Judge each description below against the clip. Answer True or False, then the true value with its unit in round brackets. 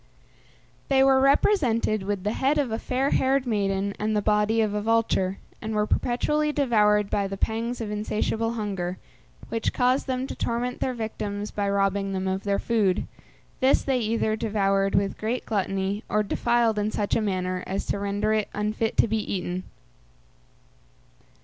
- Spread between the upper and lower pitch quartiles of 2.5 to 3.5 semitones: True (2.8 semitones)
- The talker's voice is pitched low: False (215 Hz)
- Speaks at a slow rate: False (170 wpm)